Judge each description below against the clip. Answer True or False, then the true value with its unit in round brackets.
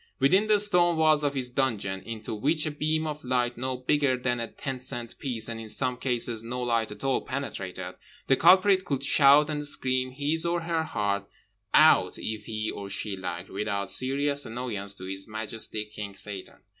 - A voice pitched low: True (125 Hz)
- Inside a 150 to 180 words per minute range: False (190 wpm)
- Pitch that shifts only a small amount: False (5.2 semitones)